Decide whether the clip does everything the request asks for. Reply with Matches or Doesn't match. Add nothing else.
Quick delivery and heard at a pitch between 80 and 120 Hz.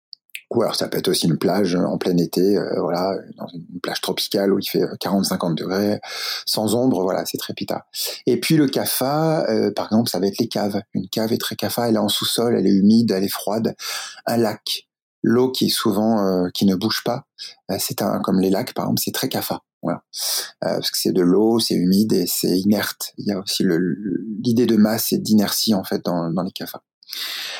Matches